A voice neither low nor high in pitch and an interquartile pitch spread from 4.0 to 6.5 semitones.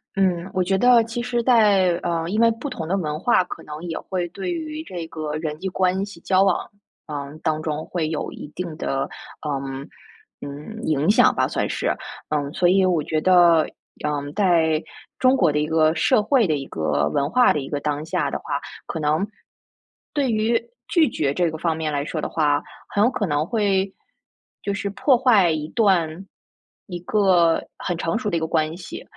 Yes: medium, 175 Hz; average, 4.8 semitones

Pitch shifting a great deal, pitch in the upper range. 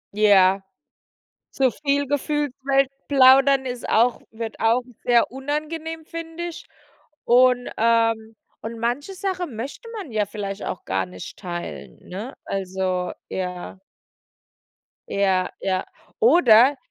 Yes: wide, 6.1 semitones; high, 240 Hz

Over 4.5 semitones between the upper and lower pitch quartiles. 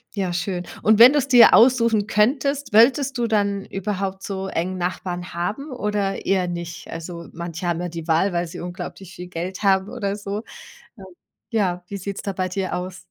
No: average, 3.2 semitones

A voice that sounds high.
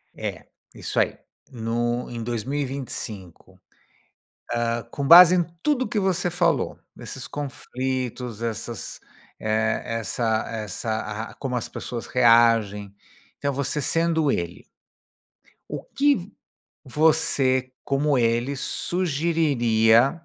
No: low, 125 Hz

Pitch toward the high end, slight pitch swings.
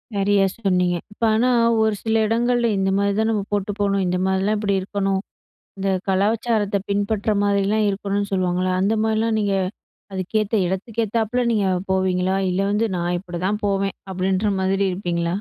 Yes: high, 200 Hz; narrow, 2.2 semitones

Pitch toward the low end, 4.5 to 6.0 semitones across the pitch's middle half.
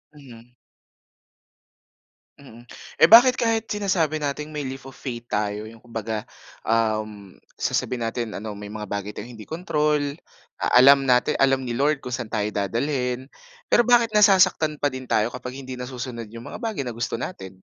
Yes: low, 125 Hz; average, 4.8 semitones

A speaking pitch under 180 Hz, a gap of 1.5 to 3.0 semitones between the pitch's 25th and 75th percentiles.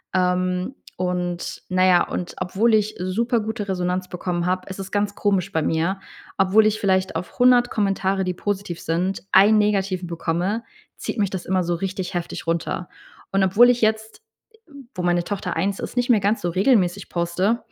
No: high, 190 Hz; narrow, 2.5 semitones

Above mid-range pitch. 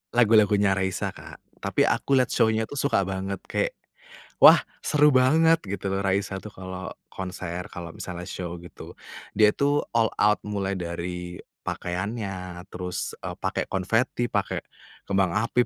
No: very low, 95 Hz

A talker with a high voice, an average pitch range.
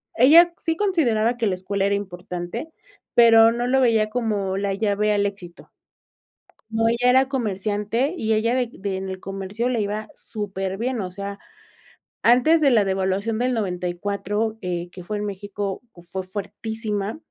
Yes: high, 210 Hz; average, 3.3 semitones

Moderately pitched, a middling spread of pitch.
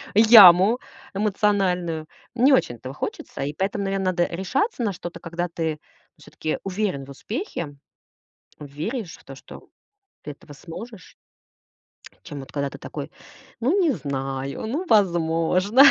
No: medium, 180 Hz; wide, 6.1 semitones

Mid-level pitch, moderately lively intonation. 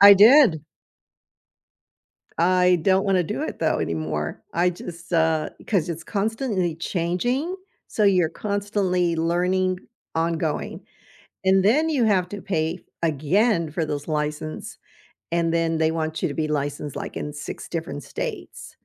Yes: medium, 170 Hz; average, 3.6 semitones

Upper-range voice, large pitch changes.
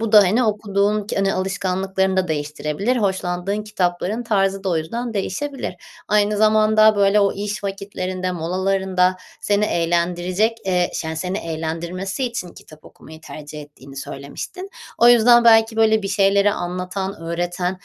No: high, 195 Hz; average, 3.1 semitones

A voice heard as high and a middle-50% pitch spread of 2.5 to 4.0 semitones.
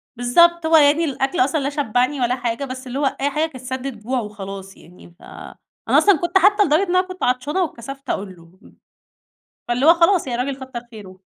No: very high, 265 Hz; average, 4.8 semitones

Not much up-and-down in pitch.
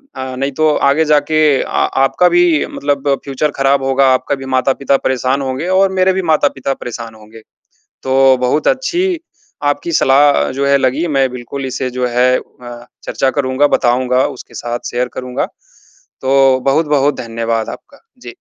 Yes: narrow, 2.3 semitones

